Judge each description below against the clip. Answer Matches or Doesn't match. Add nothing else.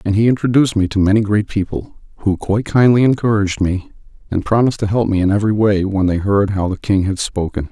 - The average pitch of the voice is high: Doesn't match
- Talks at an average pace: Doesn't match